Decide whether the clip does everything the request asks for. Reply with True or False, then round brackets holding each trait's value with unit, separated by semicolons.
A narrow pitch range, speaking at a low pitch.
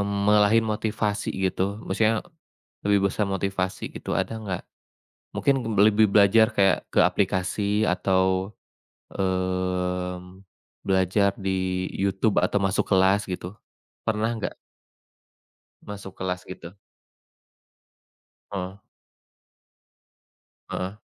True (1.9 semitones; 95 Hz)